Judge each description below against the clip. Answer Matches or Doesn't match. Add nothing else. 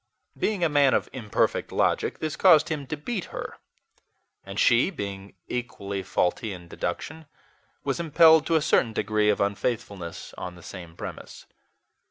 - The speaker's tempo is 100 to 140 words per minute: Doesn't match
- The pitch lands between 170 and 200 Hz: Doesn't match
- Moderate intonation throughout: Doesn't match